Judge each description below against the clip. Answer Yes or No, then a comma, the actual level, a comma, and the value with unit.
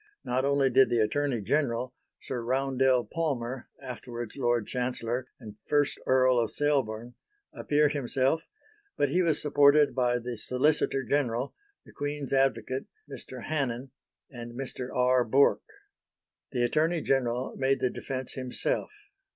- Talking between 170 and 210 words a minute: No, slow, 135 wpm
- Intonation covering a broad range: No, average, 2.7 semitones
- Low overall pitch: Yes, low, 130 Hz